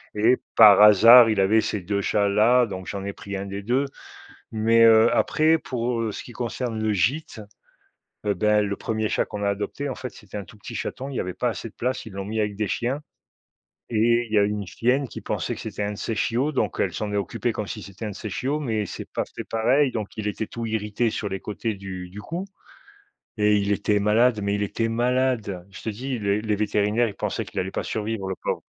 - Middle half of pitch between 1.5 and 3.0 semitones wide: Yes, narrow, 2.6 semitones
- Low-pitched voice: Yes, low, 110 Hz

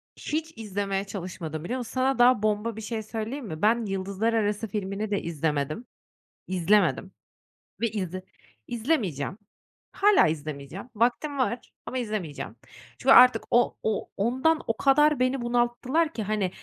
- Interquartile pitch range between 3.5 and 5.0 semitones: Yes, average, 4.5 semitones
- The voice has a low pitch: No, high, 215 Hz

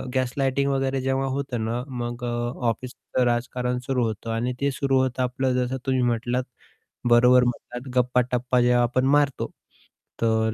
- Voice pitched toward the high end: No, low, 125 Hz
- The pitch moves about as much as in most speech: No, narrow, 1.5 semitones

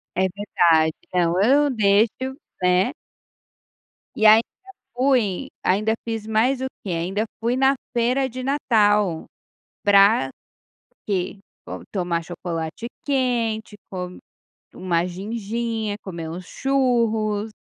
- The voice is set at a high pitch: Yes, high, 215 Hz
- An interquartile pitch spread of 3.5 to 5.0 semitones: Yes, average, 4.6 semitones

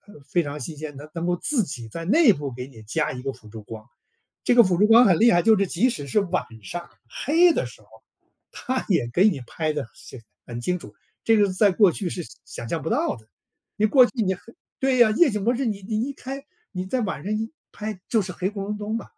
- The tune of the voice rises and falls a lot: Yes, wide, 6.9 semitones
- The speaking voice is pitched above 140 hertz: Yes, high, 190 Hz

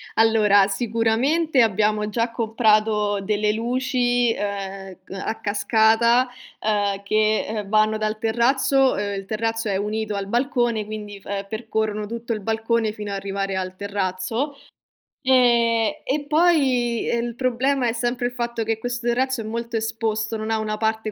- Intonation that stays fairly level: Yes, narrow, 2.2 semitones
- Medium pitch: No, high, 220 Hz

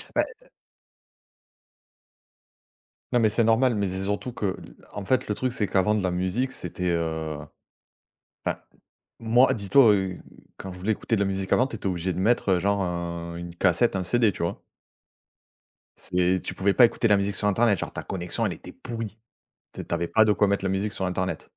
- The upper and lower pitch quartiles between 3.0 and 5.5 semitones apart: Yes, average, 3.5 semitones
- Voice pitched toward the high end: No, low, 100 Hz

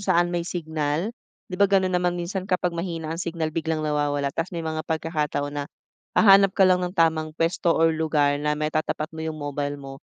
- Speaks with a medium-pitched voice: Yes, medium, 160 Hz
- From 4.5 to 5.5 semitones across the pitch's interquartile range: No, average, 2.7 semitones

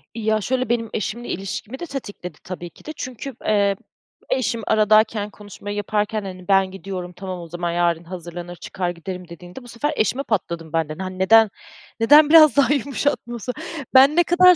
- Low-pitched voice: No, high, 205 Hz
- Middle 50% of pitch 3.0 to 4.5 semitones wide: No, wide, 5.4 semitones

